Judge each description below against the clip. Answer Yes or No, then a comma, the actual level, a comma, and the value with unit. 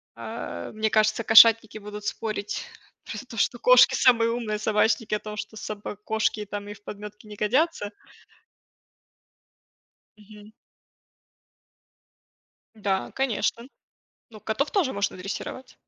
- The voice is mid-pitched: No, high, 215 Hz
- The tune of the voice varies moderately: No, narrow, 1.6 semitones